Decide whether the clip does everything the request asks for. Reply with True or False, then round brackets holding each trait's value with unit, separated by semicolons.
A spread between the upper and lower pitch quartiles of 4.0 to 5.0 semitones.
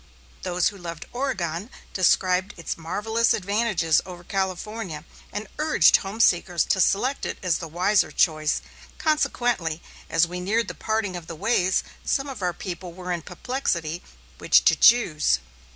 True (4.5 semitones)